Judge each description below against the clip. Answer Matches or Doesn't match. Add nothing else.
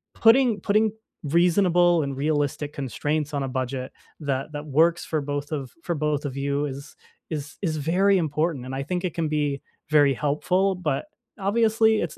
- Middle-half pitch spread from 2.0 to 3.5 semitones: Doesn't match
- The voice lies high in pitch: Doesn't match